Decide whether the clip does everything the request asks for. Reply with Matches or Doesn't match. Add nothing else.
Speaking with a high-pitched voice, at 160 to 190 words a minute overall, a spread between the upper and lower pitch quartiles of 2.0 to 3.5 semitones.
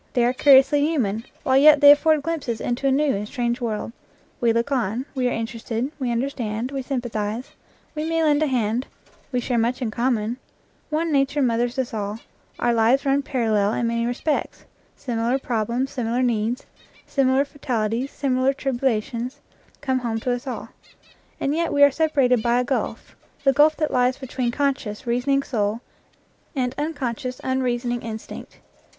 Matches